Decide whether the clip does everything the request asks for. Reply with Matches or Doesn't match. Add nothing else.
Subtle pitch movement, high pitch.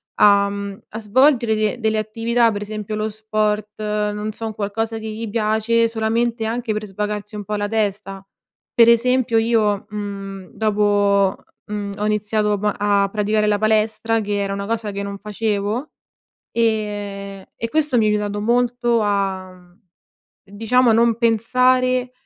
Matches